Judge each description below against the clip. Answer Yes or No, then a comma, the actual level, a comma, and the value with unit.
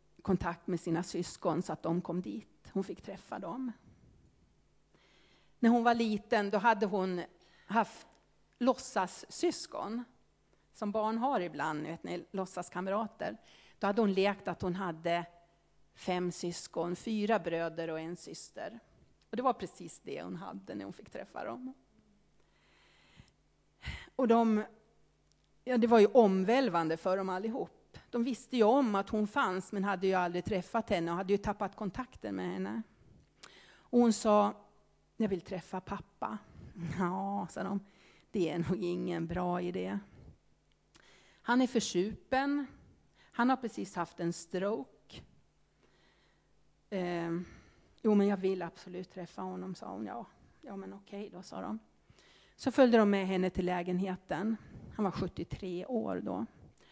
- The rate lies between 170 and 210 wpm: No, average, 145 wpm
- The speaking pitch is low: No, high, 190 Hz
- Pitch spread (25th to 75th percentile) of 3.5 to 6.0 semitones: Yes, average, 3.8 semitones